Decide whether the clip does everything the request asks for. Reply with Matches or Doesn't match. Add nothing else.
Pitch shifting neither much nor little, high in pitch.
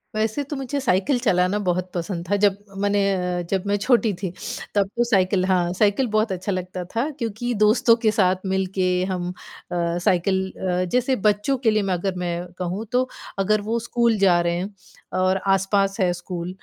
Matches